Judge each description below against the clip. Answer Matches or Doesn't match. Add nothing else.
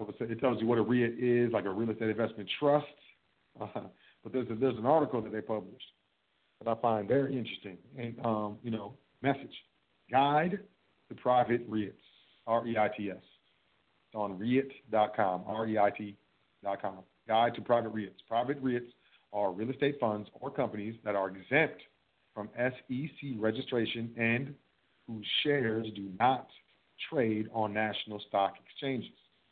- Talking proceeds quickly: Doesn't match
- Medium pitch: Doesn't match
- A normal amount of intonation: Matches